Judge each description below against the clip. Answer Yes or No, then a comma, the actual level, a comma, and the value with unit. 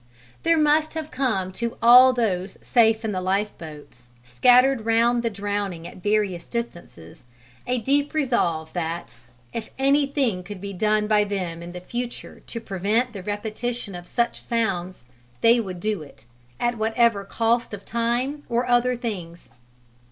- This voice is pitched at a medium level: No, high, 220 Hz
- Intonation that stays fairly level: No, average, 4.5 semitones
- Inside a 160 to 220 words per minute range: No, average, 150 wpm